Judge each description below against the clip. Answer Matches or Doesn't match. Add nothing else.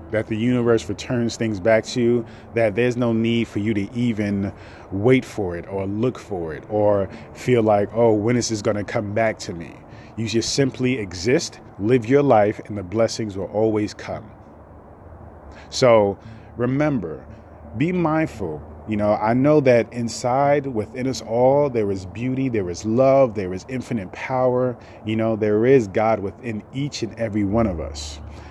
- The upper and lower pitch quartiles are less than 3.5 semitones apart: Matches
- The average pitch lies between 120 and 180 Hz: Doesn't match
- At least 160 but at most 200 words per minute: Matches